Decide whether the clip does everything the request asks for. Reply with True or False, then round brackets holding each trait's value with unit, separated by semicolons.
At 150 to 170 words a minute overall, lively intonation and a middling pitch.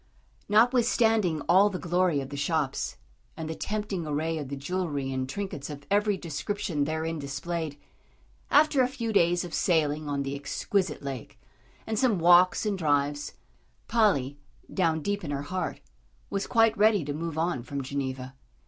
True (160 wpm; 5.9 semitones; 165 Hz)